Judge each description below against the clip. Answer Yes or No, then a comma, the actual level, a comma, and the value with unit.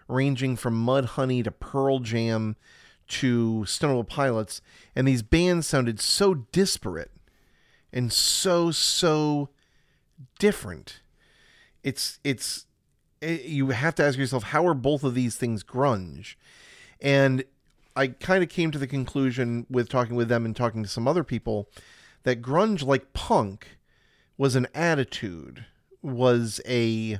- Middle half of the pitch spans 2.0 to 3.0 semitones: No, average, 3.5 semitones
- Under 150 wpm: Yes, slow, 135 wpm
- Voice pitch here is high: No, low, 130 Hz